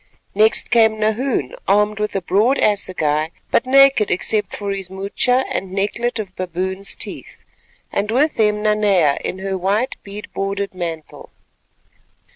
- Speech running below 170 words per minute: Yes, average, 140 wpm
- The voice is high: Yes, high, 200 Hz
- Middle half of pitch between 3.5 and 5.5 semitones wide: No, narrow, 2.5 semitones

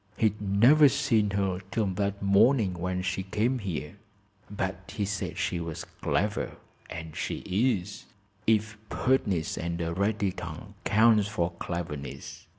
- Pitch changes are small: No, average, 3.3 semitones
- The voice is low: Yes, low, 100 Hz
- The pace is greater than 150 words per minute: No, average, 140 wpm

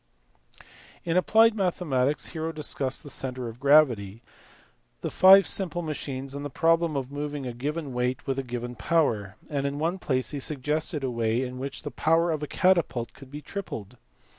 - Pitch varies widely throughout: No, average, 4.3 semitones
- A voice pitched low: No, medium, 145 Hz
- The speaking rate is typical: Yes, average, 180 wpm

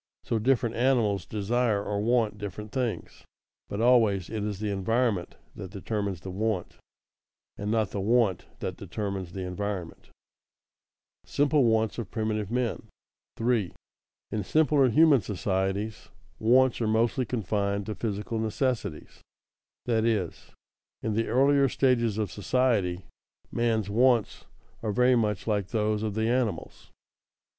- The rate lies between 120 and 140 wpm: Yes, slow, 135 wpm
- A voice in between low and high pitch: No, low, 110 Hz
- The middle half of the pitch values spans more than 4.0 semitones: No, average, 3.0 semitones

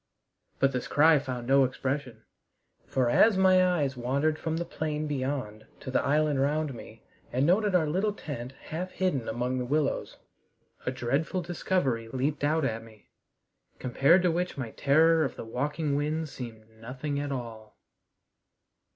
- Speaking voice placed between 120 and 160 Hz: Yes, medium, 140 Hz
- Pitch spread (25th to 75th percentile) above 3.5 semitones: Yes, average, 4.0 semitones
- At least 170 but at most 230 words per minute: No, average, 160 wpm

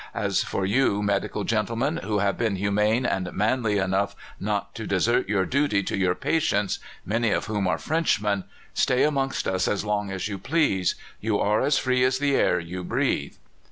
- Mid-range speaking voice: No, low, 105 Hz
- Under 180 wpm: No, average, 185 wpm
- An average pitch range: Yes, average, 4.2 semitones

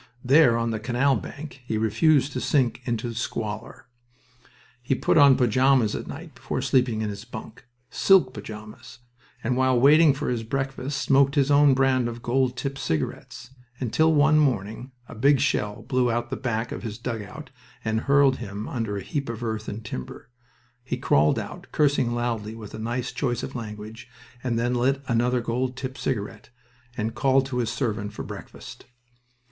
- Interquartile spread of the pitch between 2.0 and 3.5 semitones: Yes, average, 3.1 semitones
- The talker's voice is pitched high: No, low, 120 Hz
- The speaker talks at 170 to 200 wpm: Yes, average, 175 wpm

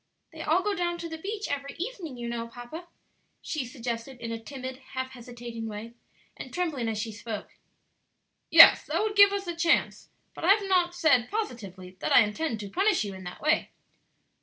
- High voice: Yes, very high, 260 Hz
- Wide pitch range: Yes, wide, 7.1 semitones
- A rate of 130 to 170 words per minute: No, average, 195 wpm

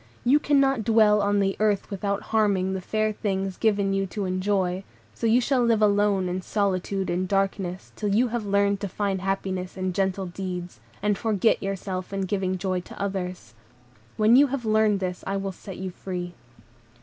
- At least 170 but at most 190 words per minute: Yes, average, 185 wpm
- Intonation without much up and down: Yes, narrow, 2.2 semitones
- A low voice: No, high, 195 Hz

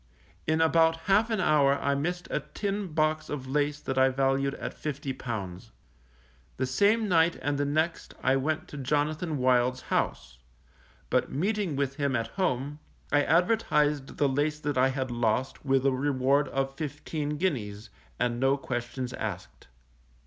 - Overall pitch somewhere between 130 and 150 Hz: Yes, medium, 140 Hz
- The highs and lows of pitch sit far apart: No, average, 3.1 semitones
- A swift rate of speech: No, average, 155 wpm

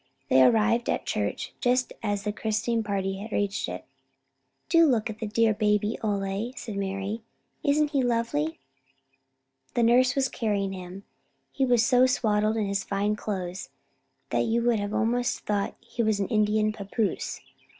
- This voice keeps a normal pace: Yes, average, 160 wpm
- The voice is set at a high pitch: Yes, high, 215 Hz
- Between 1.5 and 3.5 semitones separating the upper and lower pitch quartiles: Yes, average, 2.9 semitones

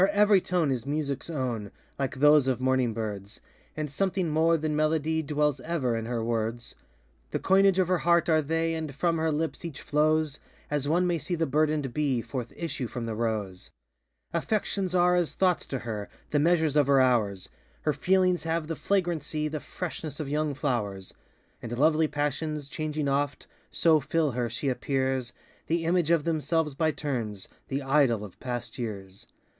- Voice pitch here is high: No, medium, 150 Hz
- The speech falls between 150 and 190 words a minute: Yes, average, 180 wpm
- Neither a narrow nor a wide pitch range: Yes, average, 4.3 semitones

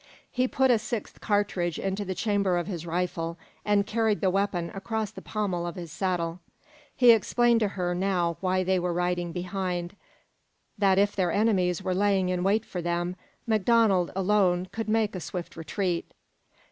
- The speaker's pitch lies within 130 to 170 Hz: No, high, 190 Hz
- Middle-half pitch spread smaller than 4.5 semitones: Yes, average, 2.8 semitones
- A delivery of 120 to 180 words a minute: Yes, average, 170 wpm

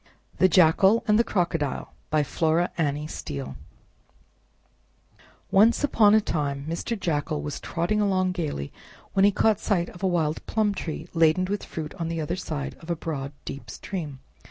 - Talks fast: No, average, 165 wpm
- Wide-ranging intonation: No, average, 4.2 semitones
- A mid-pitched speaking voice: Yes, medium, 170 Hz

